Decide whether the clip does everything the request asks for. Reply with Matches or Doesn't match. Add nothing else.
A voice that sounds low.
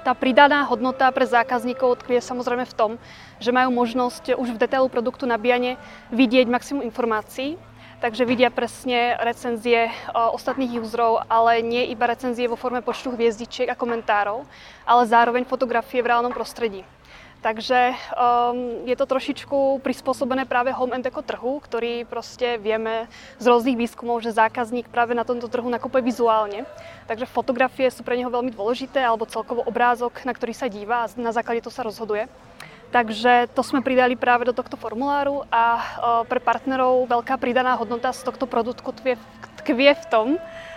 Doesn't match